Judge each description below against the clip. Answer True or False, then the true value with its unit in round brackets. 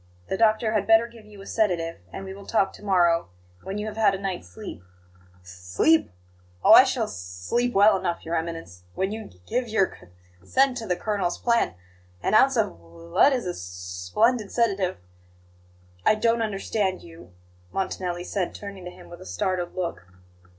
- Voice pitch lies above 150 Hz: True (190 Hz)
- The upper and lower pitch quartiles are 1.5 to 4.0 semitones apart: False (4.7 semitones)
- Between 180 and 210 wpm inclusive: True (190 wpm)